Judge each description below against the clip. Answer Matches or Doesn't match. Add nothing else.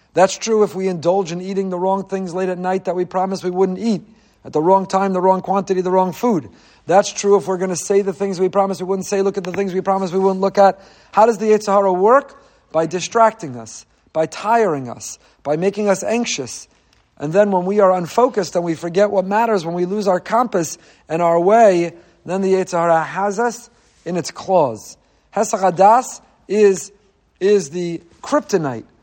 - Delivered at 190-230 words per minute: Matches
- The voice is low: Doesn't match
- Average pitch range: Doesn't match